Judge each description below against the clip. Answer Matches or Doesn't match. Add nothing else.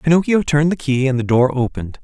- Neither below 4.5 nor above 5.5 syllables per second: Doesn't match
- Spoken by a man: Matches